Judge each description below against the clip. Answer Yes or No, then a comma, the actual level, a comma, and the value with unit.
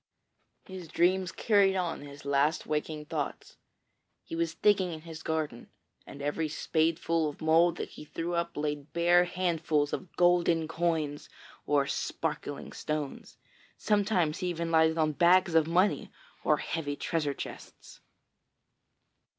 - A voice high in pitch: No, medium, 165 Hz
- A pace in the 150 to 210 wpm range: No, slow, 135 wpm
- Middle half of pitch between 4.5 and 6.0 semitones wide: No, narrow, 2.5 semitones